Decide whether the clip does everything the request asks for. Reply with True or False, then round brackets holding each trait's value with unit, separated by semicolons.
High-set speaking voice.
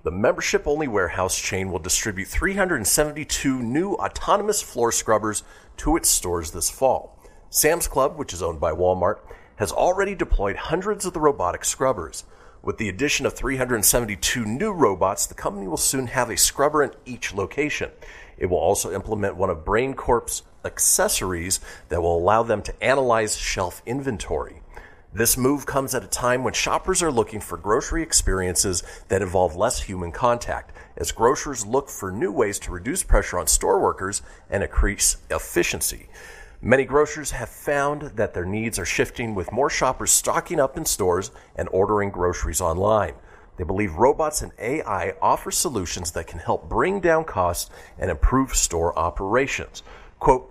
False (115 Hz)